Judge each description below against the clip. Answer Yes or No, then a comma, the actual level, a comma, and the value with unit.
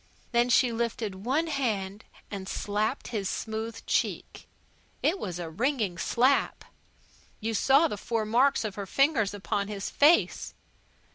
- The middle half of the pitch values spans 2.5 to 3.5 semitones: No, average, 4.5 semitones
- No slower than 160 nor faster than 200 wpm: No, average, 140 wpm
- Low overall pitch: No, high, 225 Hz